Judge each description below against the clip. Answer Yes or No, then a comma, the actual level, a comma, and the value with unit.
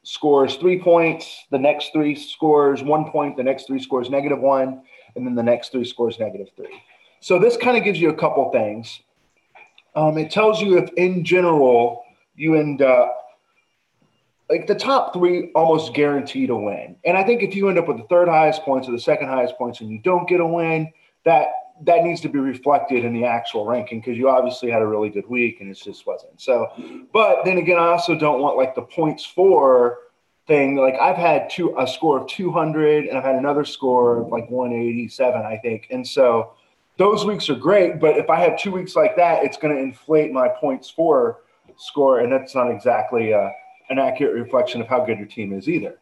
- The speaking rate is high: Yes, fast, 215 wpm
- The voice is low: No, medium, 150 Hz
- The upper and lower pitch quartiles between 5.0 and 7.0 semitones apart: Yes, wide, 5.5 semitones